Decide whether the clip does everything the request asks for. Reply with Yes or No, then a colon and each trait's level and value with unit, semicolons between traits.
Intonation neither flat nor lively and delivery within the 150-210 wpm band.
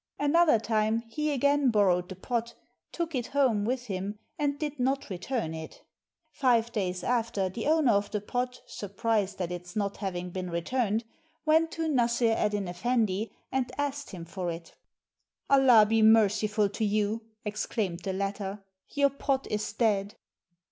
Yes: average, 4.7 semitones; average, 155 wpm